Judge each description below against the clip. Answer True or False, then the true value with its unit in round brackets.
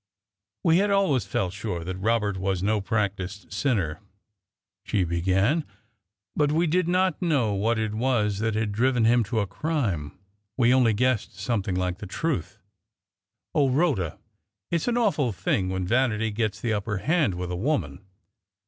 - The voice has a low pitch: True (110 Hz)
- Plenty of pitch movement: True (5.9 semitones)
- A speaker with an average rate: True (160 wpm)